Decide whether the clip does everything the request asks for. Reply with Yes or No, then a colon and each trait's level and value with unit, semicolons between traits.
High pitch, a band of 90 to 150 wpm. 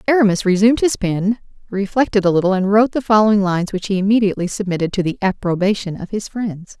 No: high, 200 Hz; average, 195 wpm